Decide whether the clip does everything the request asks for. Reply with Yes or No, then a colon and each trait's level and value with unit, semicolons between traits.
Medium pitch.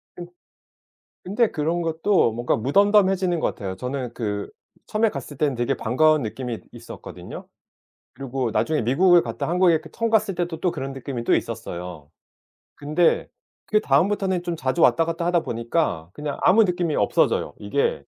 Yes: medium, 155 Hz